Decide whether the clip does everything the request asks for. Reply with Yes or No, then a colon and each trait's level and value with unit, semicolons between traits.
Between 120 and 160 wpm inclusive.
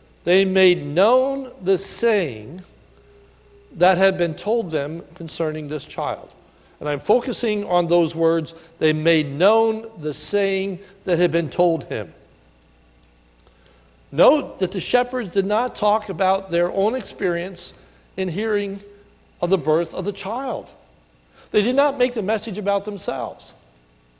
Yes: average, 140 wpm